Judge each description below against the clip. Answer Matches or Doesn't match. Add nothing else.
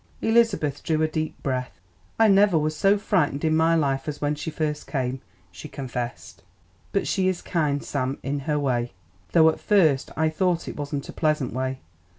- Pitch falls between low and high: Matches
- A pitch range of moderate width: Matches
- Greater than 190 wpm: Doesn't match